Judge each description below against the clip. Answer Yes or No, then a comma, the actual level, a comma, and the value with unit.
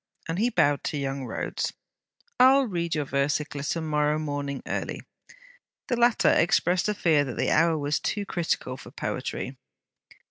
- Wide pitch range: No, average, 3.8 semitones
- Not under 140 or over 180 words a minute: Yes, average, 165 wpm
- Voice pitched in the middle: Yes, medium, 155 Hz